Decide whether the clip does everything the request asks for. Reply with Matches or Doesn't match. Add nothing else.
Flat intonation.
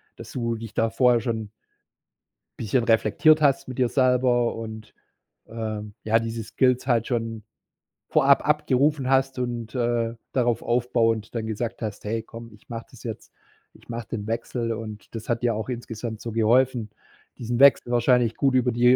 Matches